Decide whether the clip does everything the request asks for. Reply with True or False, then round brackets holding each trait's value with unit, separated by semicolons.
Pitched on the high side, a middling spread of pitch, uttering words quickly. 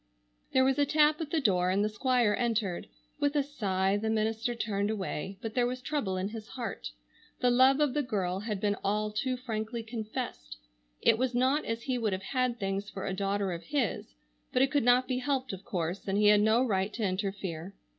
True (220 Hz; 4.5 semitones; 215 wpm)